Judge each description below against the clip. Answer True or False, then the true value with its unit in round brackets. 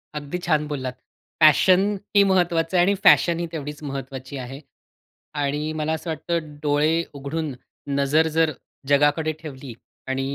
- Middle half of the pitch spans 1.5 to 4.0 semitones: True (2.7 semitones)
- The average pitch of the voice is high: False (150 Hz)